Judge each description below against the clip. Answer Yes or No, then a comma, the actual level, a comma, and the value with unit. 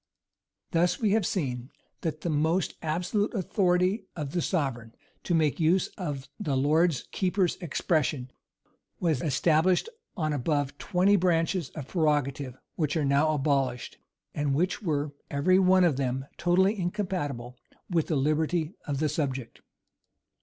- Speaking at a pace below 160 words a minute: Yes, average, 140 wpm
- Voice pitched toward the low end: No, medium, 155 Hz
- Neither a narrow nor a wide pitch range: Yes, average, 4.1 semitones